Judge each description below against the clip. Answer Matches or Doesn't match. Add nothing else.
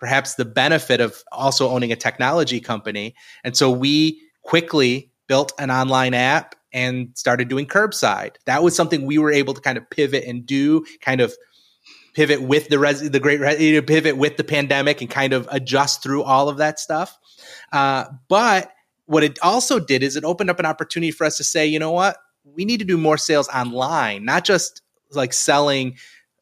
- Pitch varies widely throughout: Doesn't match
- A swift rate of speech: Doesn't match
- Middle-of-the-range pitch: Matches